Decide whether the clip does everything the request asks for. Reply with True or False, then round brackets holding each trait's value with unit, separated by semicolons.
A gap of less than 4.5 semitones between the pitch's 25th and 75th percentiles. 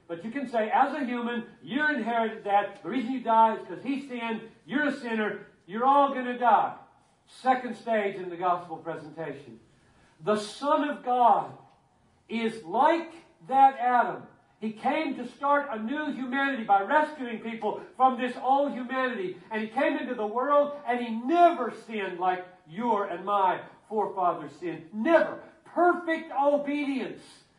False (5.1 semitones)